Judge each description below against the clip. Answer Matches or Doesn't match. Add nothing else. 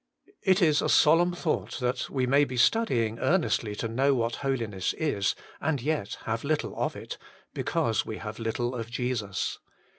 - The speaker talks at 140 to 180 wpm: Matches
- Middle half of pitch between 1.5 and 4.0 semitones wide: Doesn't match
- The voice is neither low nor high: Doesn't match